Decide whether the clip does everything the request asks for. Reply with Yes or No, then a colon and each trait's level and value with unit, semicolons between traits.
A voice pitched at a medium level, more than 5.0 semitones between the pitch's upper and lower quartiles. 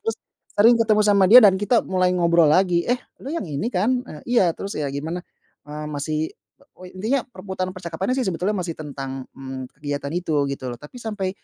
Yes: medium, 180 Hz; wide, 5.5 semitones